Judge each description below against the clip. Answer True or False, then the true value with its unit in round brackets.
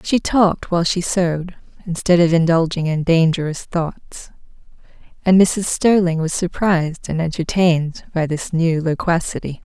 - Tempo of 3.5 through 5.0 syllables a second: True (4.7 syllables/s)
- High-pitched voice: False (170 Hz)